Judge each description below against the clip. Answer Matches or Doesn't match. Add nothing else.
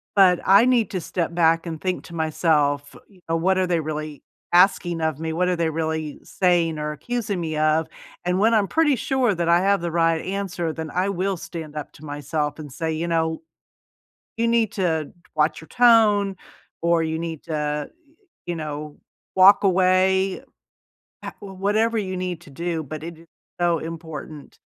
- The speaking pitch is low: Doesn't match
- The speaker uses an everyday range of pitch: Matches